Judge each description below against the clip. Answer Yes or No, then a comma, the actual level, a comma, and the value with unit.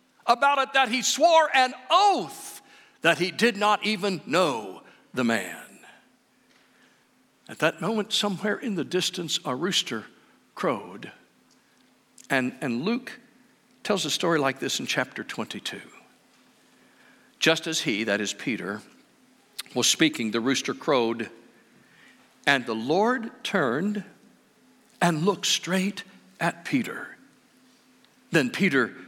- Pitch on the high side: Yes, high, 200 Hz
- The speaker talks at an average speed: No, slow, 120 wpm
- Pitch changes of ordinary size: No, wide, 7.5 semitones